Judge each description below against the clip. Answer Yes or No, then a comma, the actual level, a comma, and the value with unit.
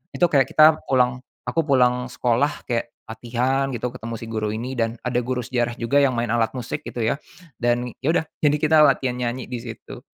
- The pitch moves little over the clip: Yes, narrow, 2.0 semitones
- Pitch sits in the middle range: No, low, 125 Hz